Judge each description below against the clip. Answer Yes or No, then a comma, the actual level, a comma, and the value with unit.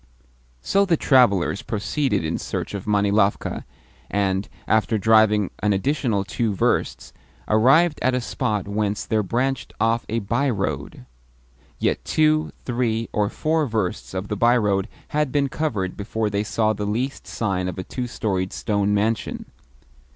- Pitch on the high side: No, low, 110 Hz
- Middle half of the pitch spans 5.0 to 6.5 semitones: No, average, 3.8 semitones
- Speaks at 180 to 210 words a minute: No, average, 150 wpm